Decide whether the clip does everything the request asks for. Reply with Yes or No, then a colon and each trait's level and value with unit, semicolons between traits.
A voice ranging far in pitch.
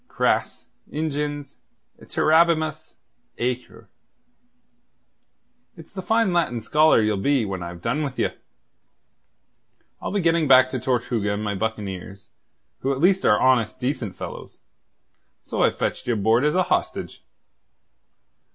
Yes: wide, 6.3 semitones